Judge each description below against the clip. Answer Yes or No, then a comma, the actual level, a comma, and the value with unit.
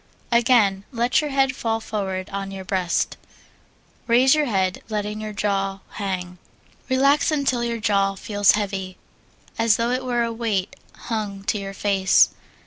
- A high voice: Yes, high, 210 Hz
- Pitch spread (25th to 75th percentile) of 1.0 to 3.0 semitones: No, average, 3.4 semitones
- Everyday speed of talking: Yes, average, 150 wpm